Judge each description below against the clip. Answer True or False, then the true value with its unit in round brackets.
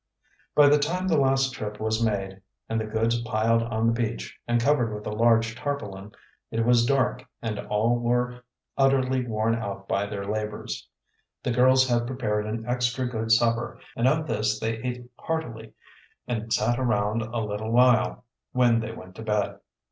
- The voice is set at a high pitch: False (115 Hz)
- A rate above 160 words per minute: True (180 wpm)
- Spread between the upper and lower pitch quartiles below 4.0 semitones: True (2.4 semitones)